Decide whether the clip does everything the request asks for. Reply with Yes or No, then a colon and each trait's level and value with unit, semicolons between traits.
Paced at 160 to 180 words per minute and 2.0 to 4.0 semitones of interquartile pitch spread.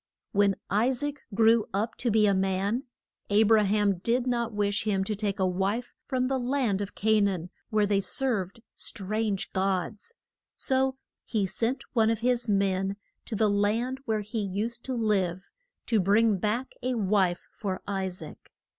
Yes: average, 175 wpm; average, 3.0 semitones